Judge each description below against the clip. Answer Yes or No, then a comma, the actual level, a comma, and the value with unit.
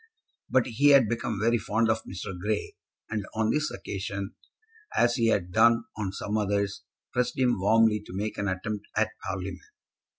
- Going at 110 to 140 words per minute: No, average, 170 wpm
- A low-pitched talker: Yes, low, 110 Hz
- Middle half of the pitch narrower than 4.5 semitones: Yes, average, 2.9 semitones